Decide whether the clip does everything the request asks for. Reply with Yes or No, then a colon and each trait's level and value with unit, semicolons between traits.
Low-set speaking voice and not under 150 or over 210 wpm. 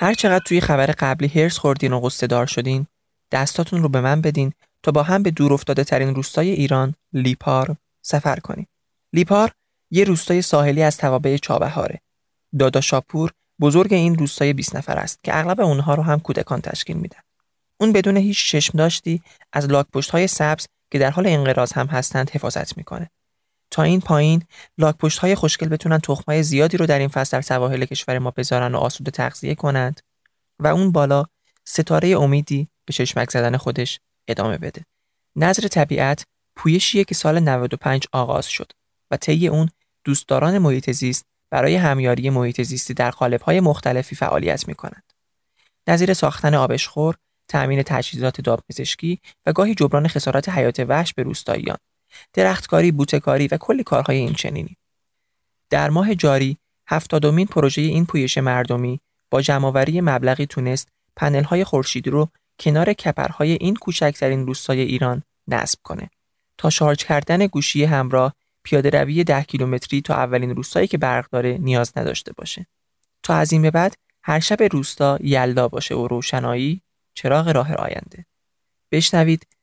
No: medium, 145 Hz; fast, 155 wpm